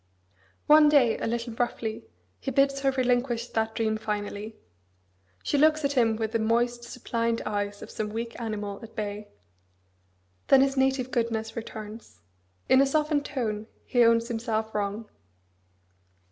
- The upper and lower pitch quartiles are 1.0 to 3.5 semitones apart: Yes, average, 3.1 semitones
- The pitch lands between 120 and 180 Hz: No, high, 230 Hz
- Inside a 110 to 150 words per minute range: Yes, average, 145 wpm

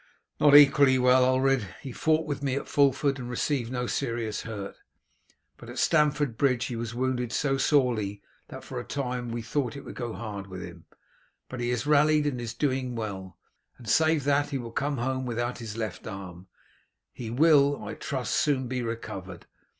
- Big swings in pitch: No, average, 3.5 semitones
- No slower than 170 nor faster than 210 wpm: Yes, average, 190 wpm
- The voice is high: No, low, 125 Hz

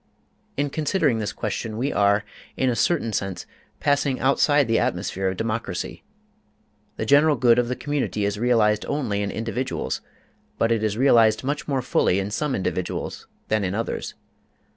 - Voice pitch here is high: No, low, 115 Hz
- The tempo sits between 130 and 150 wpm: No, average, 165 wpm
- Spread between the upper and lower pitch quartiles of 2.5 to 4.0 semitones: No, average, 4.8 semitones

